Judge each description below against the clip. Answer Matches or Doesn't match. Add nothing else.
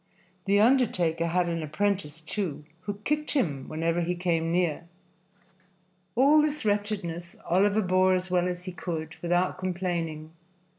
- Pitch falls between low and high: Matches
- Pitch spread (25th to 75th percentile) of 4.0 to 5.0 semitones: Doesn't match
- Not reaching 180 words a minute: Matches